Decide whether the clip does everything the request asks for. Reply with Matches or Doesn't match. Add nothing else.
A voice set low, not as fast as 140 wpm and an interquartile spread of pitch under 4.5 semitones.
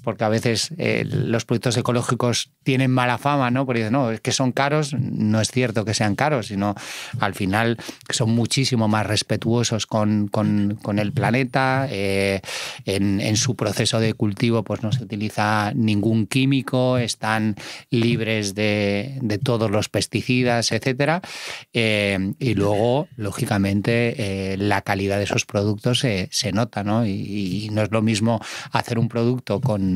Doesn't match